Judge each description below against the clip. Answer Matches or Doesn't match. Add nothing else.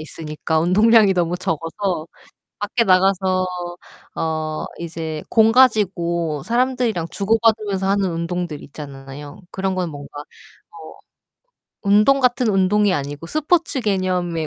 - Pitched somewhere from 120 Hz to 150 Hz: Doesn't match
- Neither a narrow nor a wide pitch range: Matches